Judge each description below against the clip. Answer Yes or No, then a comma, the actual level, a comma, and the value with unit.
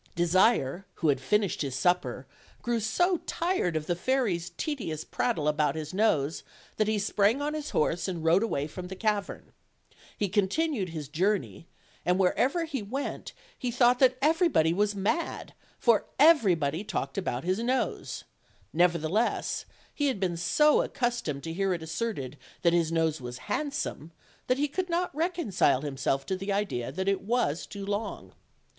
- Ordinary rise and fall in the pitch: No, wide, 7.0 semitones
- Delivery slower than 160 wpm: No, average, 165 wpm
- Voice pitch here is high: Yes, high, 195 Hz